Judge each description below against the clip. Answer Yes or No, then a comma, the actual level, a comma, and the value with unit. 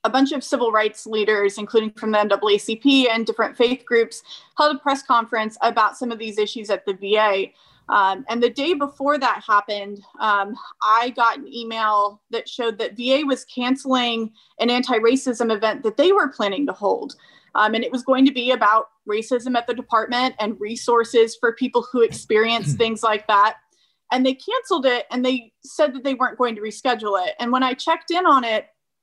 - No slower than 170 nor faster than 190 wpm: No, average, 200 wpm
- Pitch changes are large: No, average, 3.1 semitones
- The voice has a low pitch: No, high, 235 Hz